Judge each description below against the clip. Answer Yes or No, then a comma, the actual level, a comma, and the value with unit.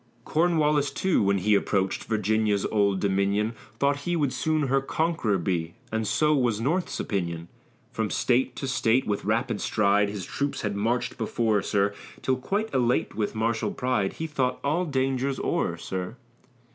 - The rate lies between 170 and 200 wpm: No, average, 160 wpm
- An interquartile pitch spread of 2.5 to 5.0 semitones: No, wide, 5.4 semitones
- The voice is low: Yes, low, 115 Hz